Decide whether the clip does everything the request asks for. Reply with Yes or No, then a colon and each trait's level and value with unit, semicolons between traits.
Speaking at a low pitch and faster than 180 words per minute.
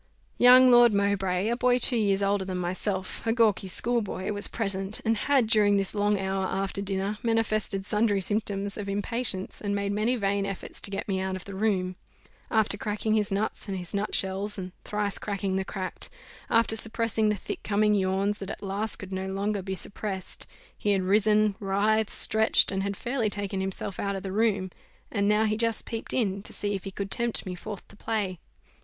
No: high, 200 Hz; average, 200 wpm